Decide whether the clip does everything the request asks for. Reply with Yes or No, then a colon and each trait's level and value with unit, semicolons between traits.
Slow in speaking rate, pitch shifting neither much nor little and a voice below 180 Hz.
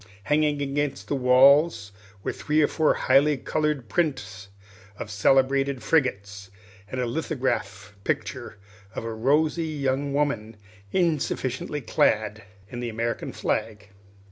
Yes: slow, 120 wpm; average, 5.0 semitones; low, 135 Hz